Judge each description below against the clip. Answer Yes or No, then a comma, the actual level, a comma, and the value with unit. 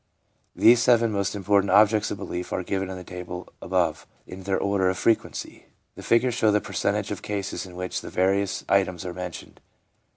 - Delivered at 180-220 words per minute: Yes, average, 190 wpm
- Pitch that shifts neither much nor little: No, narrow, 2.1 semitones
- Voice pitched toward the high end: No, low, 100 Hz